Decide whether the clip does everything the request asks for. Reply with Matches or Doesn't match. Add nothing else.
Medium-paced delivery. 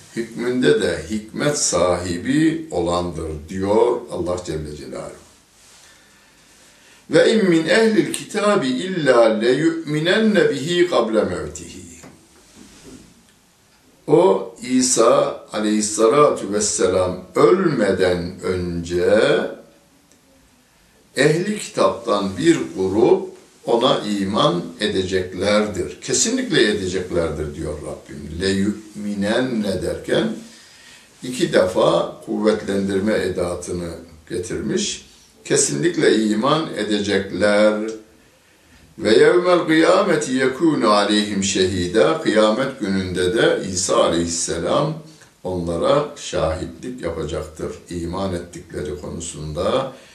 Doesn't match